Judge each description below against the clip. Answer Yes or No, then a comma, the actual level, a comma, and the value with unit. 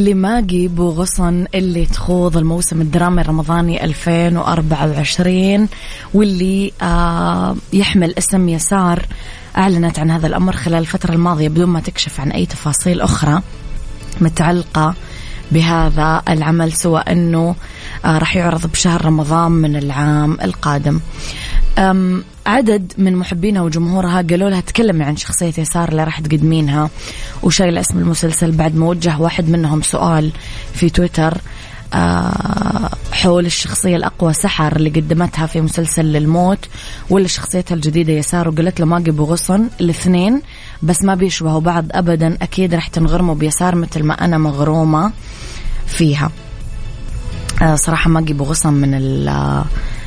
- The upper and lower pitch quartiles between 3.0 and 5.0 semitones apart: No, narrow, 2.5 semitones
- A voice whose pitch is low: No, medium, 165 Hz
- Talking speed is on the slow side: Yes, slow, 130 wpm